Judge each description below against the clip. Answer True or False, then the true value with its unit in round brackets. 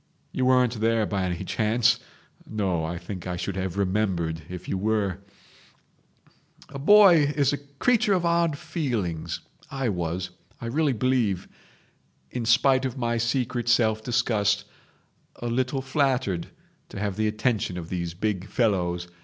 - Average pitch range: False (5.7 semitones)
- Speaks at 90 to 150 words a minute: True (145 wpm)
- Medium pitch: False (110 Hz)